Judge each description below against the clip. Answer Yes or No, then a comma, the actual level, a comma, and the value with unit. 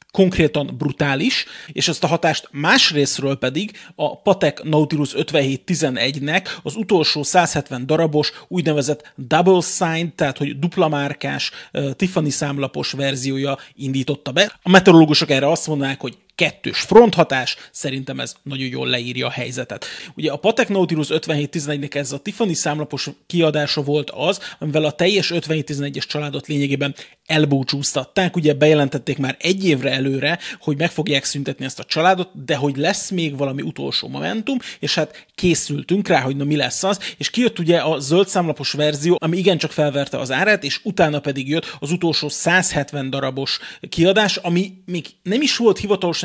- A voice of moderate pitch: Yes, medium, 155 Hz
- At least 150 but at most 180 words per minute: Yes, fast, 155 wpm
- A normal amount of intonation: Yes, average, 4.0 semitones